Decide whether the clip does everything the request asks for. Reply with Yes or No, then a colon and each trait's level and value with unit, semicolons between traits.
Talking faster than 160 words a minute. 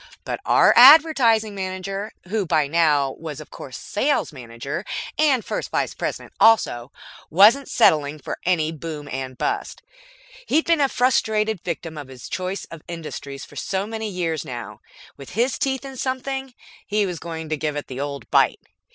Yes: average, 170 wpm